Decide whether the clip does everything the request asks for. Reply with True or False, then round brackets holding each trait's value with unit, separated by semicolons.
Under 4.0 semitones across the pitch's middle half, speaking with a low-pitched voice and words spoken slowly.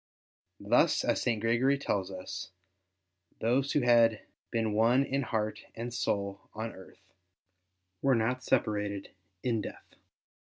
True (3.0 semitones; 115 Hz; 125 wpm)